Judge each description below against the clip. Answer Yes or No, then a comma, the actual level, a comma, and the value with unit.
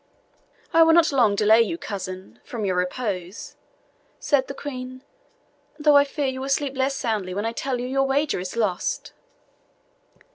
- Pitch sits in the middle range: No, very high, 255 Hz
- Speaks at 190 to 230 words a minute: No, average, 170 wpm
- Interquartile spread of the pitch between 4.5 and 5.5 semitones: Yes, average, 5.1 semitones